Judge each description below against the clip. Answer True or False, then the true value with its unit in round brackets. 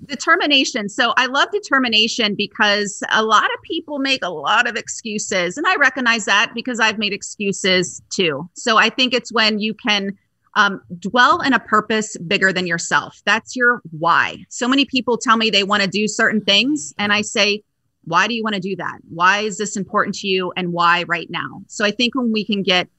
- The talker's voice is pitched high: True (215 Hz)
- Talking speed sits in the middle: False (210 wpm)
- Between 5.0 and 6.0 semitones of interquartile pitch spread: False (3.6 semitones)